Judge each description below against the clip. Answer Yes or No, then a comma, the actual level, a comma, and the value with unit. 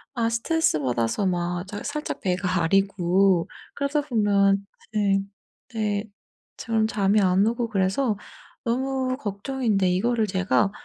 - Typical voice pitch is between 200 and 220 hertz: Yes, high, 205 Hz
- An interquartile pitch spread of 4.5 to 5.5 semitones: No, average, 3.6 semitones